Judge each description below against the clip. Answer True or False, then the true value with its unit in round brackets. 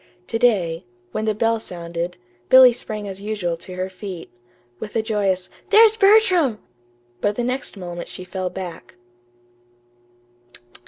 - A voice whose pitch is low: False (205 Hz)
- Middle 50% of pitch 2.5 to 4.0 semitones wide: False (4.4 semitones)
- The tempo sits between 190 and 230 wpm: False (140 wpm)